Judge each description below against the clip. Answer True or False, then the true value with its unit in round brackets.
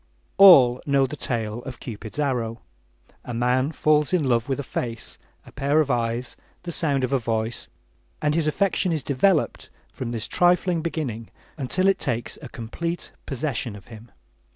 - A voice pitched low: True (130 Hz)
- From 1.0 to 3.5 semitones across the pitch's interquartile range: False (4.8 semitones)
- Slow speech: False (165 wpm)